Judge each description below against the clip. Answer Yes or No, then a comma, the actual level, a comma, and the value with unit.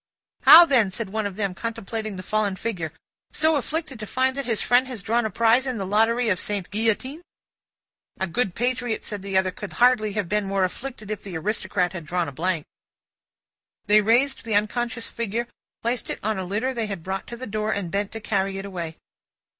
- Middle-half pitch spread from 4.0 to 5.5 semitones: No, average, 3.6 semitones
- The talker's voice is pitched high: Yes, high, 215 Hz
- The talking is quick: Yes, fast, 210 wpm